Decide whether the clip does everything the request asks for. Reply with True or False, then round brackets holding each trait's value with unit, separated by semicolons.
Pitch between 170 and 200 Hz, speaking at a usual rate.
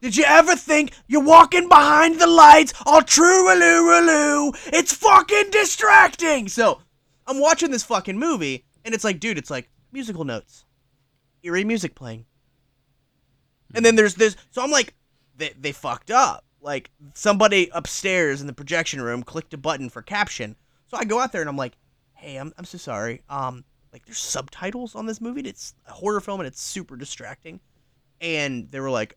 True (190 Hz; 180 wpm)